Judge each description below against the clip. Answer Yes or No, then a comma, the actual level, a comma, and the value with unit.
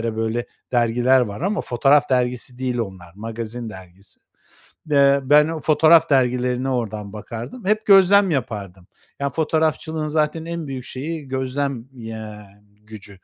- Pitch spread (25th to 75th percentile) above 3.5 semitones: Yes, average, 5.2 semitones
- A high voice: No, low, 130 Hz